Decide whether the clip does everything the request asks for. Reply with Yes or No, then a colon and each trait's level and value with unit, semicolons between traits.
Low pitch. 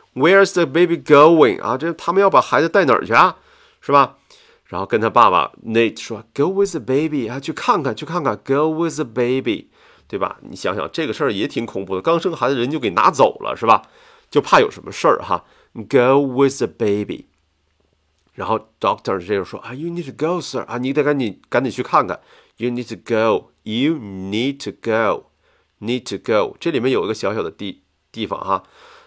No: medium, 145 Hz